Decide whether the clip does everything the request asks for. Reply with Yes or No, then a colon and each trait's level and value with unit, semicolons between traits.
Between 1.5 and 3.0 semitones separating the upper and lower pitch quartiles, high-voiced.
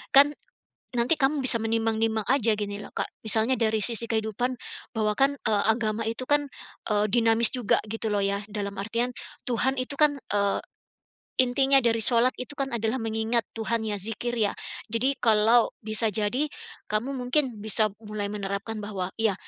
Yes: average, 2.7 semitones; high, 225 Hz